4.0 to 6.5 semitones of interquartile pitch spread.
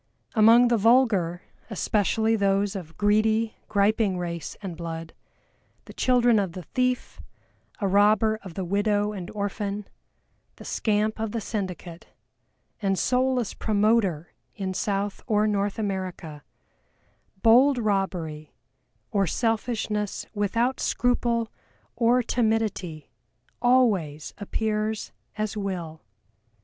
No: average, 3.0 semitones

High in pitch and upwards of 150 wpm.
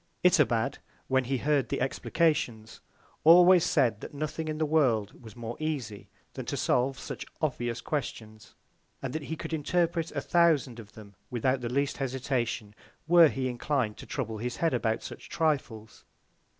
No: low, 135 Hz; average, 165 wpm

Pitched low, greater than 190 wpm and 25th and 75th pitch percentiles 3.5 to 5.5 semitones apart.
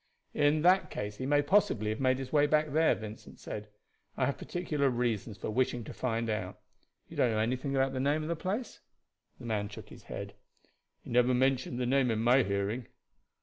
Yes: low, 130 Hz; fast, 205 wpm; average, 4.6 semitones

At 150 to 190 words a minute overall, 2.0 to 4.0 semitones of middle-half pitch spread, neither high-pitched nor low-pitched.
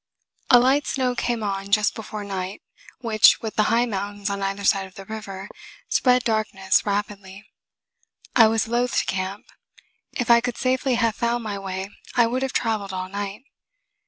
No: average, 175 wpm; average, 3.3 semitones; high, 215 Hz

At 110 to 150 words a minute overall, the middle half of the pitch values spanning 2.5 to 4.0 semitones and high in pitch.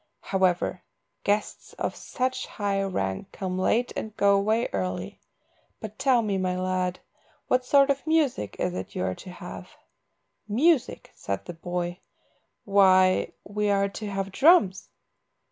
Yes: average, 145 wpm; average, 3.7 semitones; high, 195 Hz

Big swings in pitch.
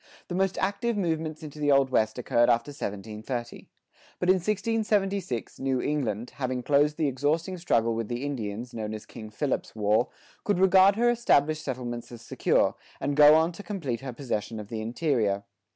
Yes: wide, 6.5 semitones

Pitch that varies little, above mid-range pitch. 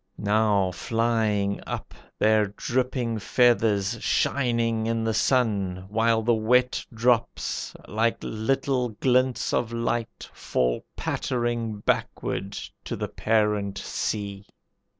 No: narrow, 2.3 semitones; low, 110 Hz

